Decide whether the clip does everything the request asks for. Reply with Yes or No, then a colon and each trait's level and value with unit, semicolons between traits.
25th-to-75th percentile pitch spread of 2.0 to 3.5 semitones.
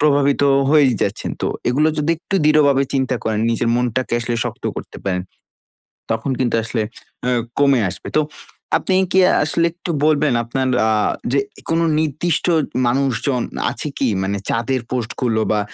No: average, 3.9 semitones